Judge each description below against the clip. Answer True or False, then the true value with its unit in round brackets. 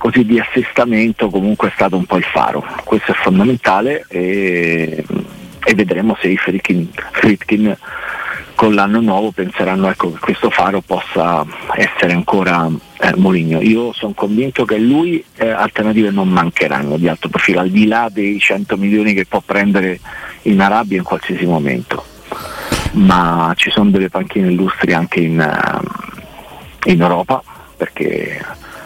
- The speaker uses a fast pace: False (145 wpm)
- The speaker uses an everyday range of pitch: True (3.5 semitones)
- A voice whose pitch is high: False (100 Hz)